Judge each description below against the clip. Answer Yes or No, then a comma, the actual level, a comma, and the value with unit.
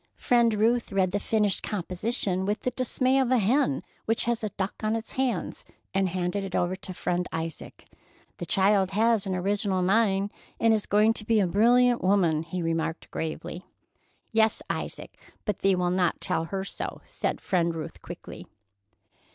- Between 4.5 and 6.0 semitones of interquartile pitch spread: No, average, 3.8 semitones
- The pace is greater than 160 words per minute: Yes, average, 175 wpm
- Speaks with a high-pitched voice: Yes, high, 195 Hz